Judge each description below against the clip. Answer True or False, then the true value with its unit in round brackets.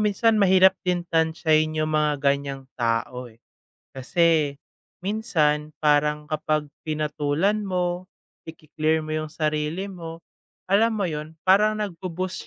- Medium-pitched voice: True (155 Hz)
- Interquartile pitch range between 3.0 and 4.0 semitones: True (3.6 semitones)